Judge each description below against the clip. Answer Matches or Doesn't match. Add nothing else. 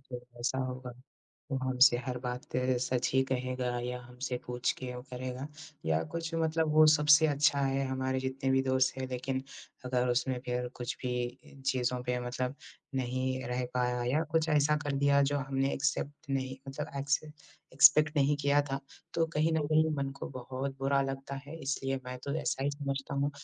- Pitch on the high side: Doesn't match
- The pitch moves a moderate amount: Doesn't match